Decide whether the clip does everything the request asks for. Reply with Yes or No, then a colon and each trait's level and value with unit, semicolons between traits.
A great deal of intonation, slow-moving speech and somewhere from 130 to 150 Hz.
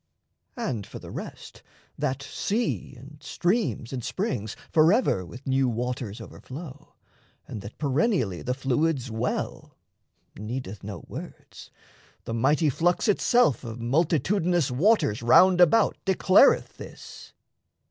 Yes: wide, 6.7 semitones; slow, 115 wpm; low, 135 Hz